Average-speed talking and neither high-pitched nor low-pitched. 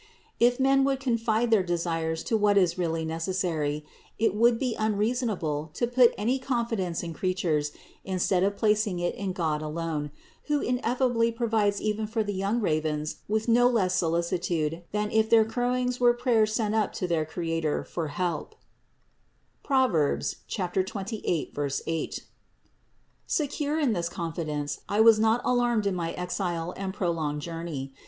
No: average, 150 wpm; high, 200 Hz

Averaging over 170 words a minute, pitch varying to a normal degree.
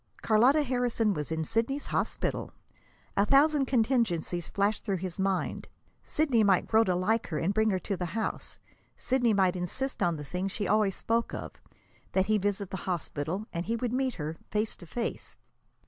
Yes: average, 180 wpm; average, 4.4 semitones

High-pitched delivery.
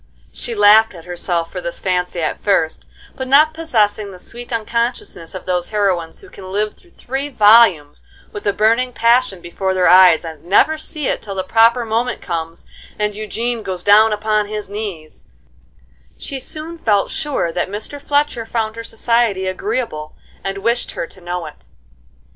Yes: high, 210 Hz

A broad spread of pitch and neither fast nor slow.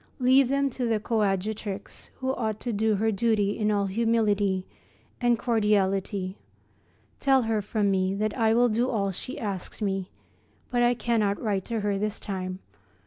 No: average, 2.8 semitones; average, 165 wpm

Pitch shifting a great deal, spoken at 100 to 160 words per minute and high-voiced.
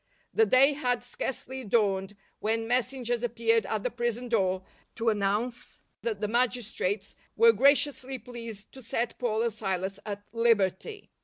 No: average, 3.0 semitones; average, 150 wpm; high, 230 Hz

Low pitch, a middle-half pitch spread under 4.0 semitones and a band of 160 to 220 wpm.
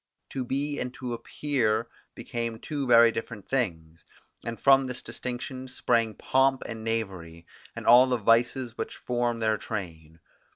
No: low, 115 Hz; average, 2.8 semitones; average, 150 wpm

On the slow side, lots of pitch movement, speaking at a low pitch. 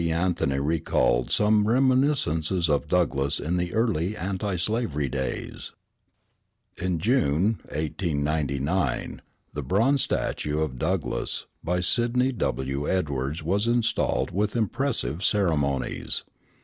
Yes: slow, 105 wpm; wide, 6.6 semitones; very low, 90 Hz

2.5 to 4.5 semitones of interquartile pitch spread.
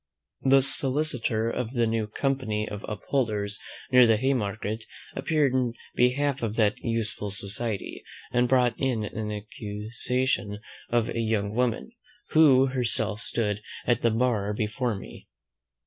Yes: average, 3.2 semitones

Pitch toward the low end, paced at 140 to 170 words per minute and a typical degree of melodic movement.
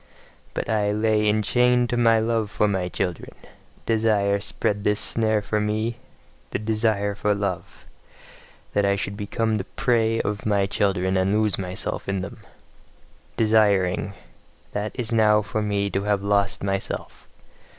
No: low, 105 Hz; average, 150 wpm; narrow, 1.7 semitones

